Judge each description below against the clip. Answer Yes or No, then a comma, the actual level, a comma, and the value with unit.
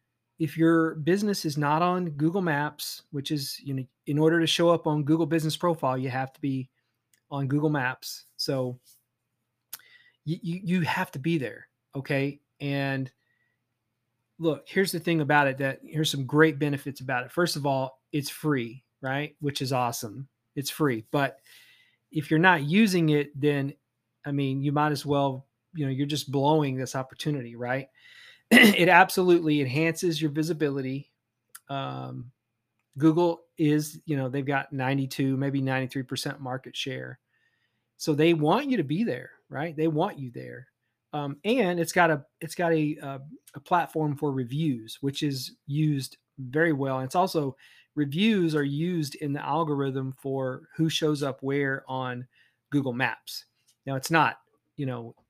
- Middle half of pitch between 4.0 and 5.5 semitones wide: No, average, 3.4 semitones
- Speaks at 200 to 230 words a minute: No, average, 165 wpm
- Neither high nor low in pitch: Yes, medium, 145 Hz